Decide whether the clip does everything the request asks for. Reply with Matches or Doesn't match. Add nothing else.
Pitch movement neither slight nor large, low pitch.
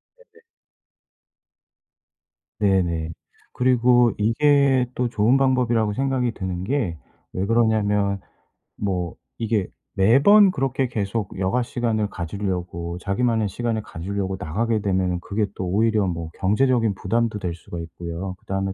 Matches